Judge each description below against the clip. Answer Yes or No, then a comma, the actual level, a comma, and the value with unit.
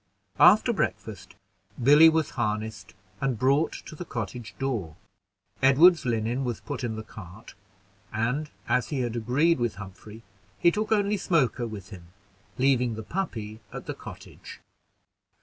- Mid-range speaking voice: No, low, 120 Hz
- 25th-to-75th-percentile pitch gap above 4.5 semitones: Yes, average, 5.1 semitones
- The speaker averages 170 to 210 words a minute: No, average, 145 wpm